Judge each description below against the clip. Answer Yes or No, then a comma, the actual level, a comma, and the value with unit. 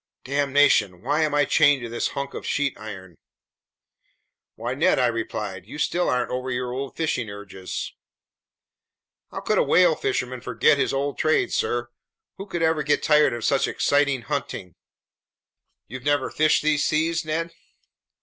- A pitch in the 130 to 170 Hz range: Yes, low, 135 Hz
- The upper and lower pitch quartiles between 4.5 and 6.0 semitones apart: No, average, 4.1 semitones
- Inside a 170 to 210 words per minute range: No, average, 160 wpm